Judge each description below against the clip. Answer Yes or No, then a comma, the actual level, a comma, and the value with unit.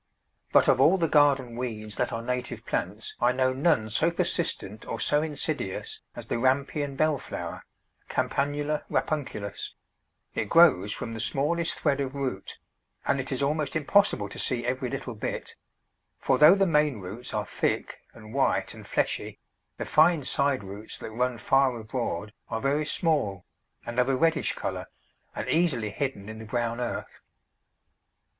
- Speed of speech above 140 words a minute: Yes, average, 165 wpm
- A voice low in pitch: Yes, low, 130 Hz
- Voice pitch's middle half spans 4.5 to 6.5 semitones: Yes, average, 4.8 semitones